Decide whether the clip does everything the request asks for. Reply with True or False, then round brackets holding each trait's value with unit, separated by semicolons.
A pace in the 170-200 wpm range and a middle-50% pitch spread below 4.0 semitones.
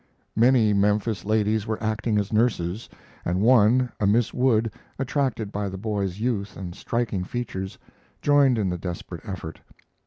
False (150 wpm; 3.2 semitones)